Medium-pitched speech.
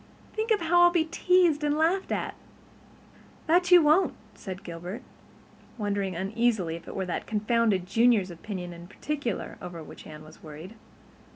No: high, 215 Hz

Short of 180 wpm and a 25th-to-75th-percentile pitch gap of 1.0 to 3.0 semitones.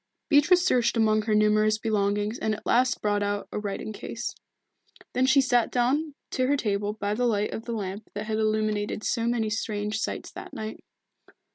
No: average, 185 wpm; narrow, 2.6 semitones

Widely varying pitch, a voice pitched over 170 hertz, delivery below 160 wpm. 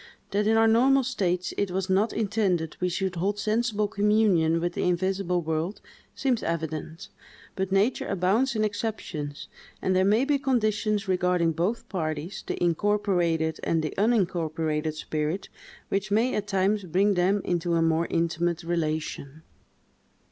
No: average, 4.0 semitones; medium, 185 Hz; average, 150 wpm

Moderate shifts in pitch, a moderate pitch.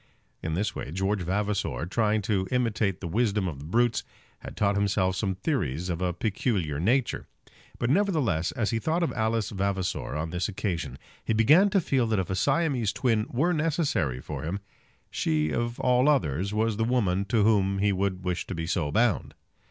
No: average, 4.5 semitones; low, 105 Hz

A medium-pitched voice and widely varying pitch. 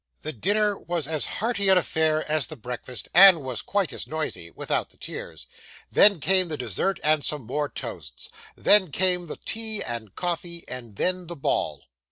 Yes: medium, 160 Hz; wide, 6.2 semitones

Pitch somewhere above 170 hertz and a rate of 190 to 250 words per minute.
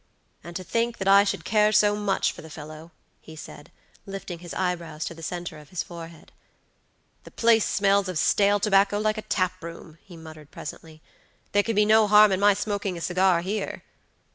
Yes: high, 190 Hz; average, 195 wpm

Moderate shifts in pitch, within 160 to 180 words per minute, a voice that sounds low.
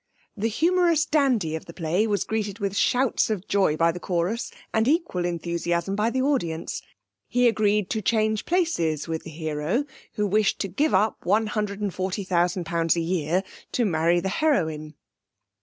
No: average, 4.7 semitones; average, 175 wpm; high, 195 Hz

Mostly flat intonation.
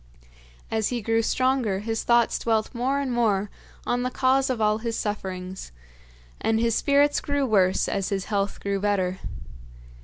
No: average, 3.8 semitones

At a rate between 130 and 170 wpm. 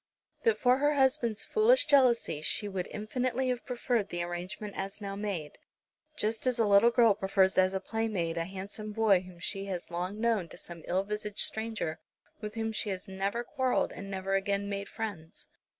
No: average, 185 wpm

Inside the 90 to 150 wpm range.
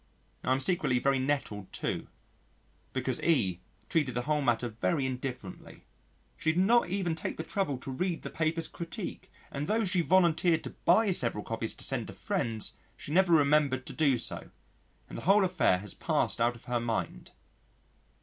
No: average, 180 wpm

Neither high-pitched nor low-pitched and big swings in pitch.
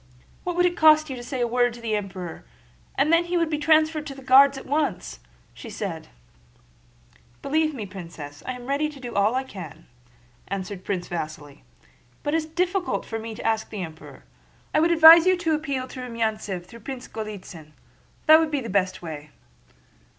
No: high, 245 Hz; wide, 8.8 semitones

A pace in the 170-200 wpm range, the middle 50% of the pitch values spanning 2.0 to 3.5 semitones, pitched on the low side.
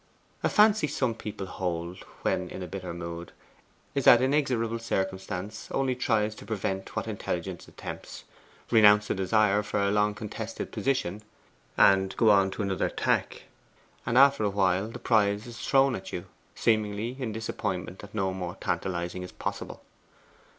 No: average, 155 wpm; average, 3.2 semitones; low, 105 Hz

